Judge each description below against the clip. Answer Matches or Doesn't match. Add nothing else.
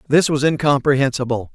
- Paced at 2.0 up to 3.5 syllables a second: Doesn't match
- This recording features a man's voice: Matches